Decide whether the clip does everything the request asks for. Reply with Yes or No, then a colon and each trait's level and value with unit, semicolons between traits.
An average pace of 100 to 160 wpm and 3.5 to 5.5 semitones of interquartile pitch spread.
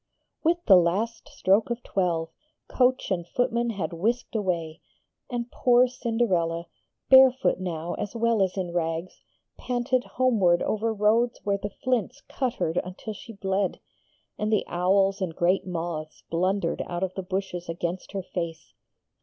Yes: average, 150 wpm; average, 5.1 semitones